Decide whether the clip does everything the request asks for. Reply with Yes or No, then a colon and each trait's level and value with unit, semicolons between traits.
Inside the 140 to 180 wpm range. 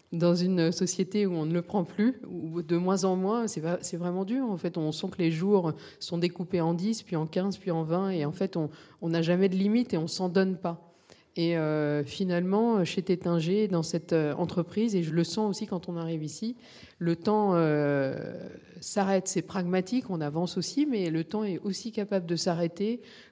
No: average, 210 wpm